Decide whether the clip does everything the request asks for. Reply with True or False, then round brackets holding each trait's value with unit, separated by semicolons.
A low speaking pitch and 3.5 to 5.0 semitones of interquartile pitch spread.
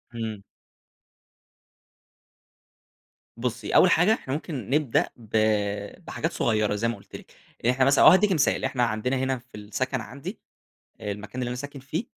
True (125 Hz; 4.0 semitones)